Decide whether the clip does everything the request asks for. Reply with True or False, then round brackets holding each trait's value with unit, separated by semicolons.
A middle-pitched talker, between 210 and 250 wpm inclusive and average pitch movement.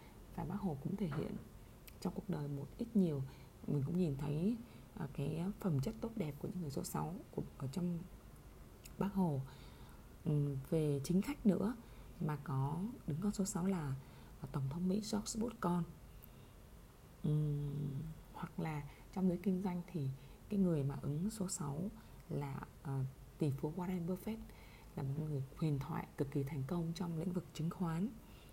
False (160 Hz; 165 wpm; 4.8 semitones)